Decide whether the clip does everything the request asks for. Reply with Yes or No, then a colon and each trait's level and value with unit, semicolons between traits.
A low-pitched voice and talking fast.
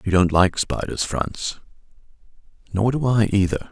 No: low, 100 Hz; average, 145 wpm